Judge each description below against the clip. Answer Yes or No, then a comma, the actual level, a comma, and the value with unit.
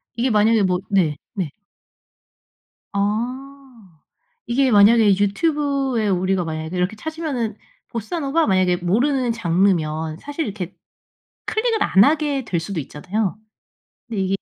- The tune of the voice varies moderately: No, wide, 6.3 semitones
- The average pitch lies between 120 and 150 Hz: No, high, 210 Hz